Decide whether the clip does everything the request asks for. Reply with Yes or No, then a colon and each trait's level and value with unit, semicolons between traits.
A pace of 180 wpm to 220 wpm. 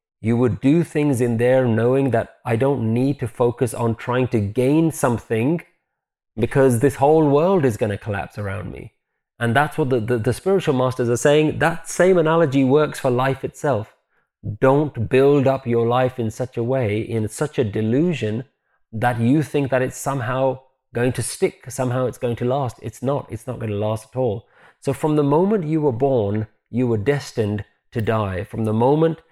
Yes: average, 195 wpm